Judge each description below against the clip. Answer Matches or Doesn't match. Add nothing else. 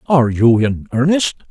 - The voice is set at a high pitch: Doesn't match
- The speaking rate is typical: Matches